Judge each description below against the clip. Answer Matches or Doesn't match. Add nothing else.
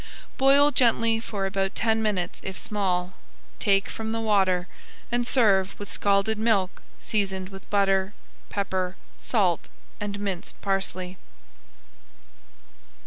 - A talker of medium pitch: Doesn't match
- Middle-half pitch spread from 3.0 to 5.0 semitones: Doesn't match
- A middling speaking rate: Doesn't match